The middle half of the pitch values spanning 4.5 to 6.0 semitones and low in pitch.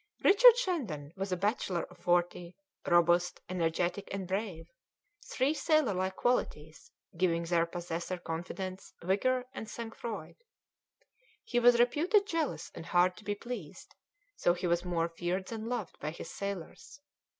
No: wide, 5.4 semitones; medium, 185 Hz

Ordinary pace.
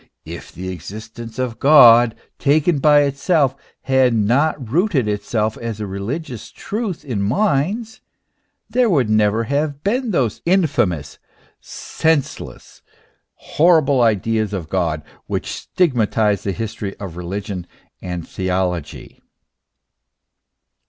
No: slow, 110 wpm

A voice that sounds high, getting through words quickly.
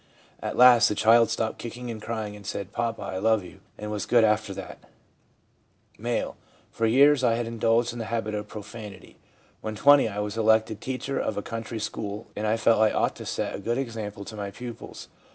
No: low, 110 Hz; fast, 210 wpm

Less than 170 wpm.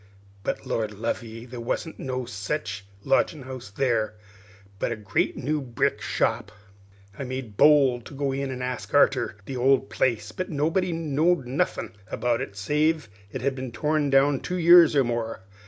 No: average, 175 wpm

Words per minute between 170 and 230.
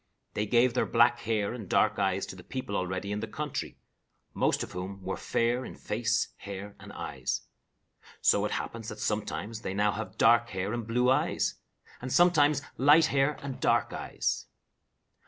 Yes: average, 175 wpm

